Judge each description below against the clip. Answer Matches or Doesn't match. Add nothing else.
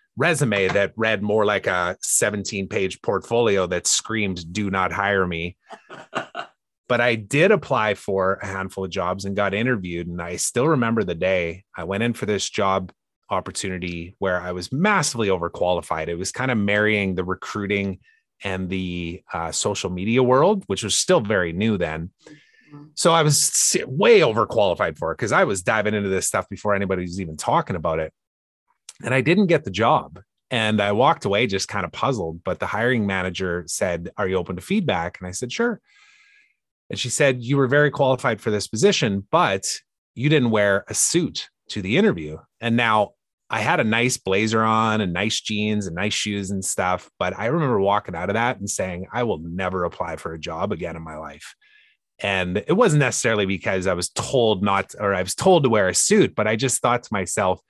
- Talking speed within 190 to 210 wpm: Matches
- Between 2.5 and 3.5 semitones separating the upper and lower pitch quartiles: Doesn't match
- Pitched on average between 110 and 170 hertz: Doesn't match